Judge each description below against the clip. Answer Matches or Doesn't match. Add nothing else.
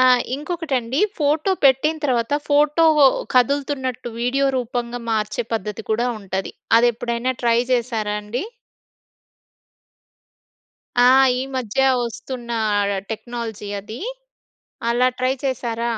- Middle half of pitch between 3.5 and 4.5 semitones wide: Doesn't match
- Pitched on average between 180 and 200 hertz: Doesn't match